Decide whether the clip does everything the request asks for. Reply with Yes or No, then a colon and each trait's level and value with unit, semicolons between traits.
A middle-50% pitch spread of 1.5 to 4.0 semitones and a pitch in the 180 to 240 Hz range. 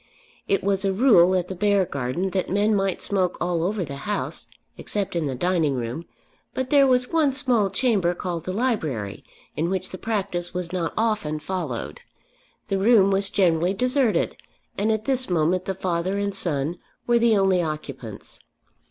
Yes: average, 3.7 semitones; high, 190 Hz